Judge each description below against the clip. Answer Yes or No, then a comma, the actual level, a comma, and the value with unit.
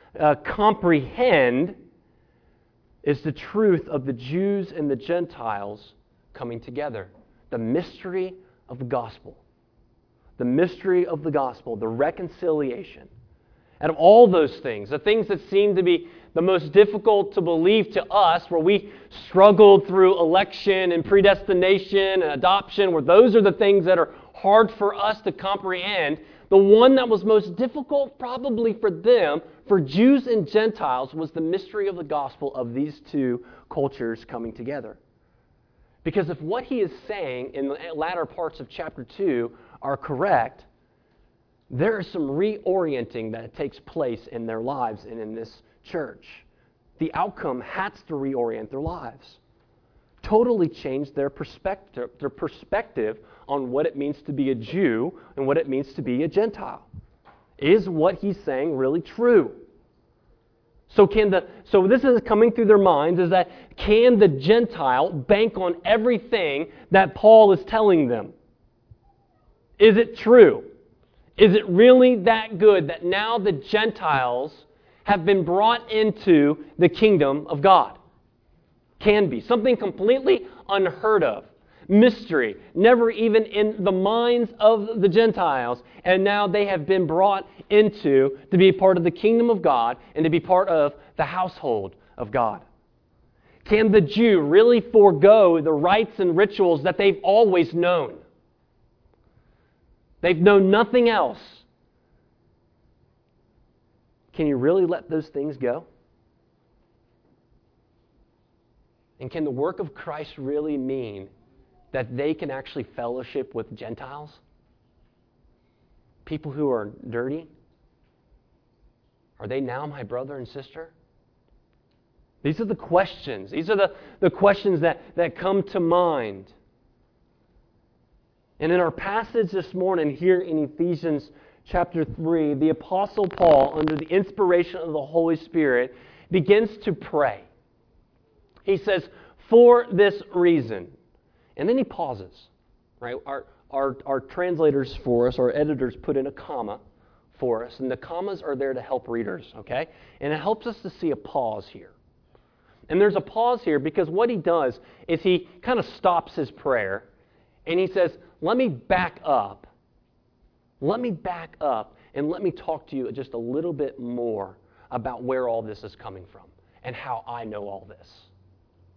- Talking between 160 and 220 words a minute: No, average, 150 wpm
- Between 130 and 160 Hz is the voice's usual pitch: No, medium, 175 Hz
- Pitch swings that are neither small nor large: No, wide, 7.0 semitones